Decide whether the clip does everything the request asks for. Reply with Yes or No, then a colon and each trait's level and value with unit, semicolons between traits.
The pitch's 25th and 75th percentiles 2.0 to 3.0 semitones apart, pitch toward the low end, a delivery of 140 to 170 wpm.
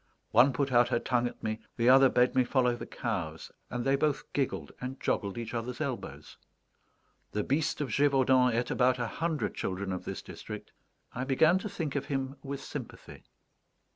No: narrow, 2.6 semitones; low, 125 Hz; average, 185 wpm